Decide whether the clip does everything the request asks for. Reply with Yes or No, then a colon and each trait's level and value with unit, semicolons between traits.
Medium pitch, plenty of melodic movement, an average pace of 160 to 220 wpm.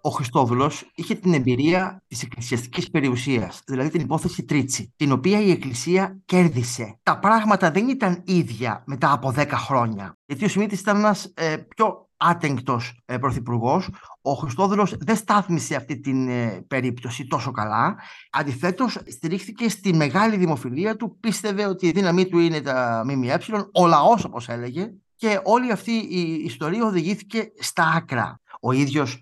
No: medium, 165 Hz; wide, 7.0 semitones; average, 150 wpm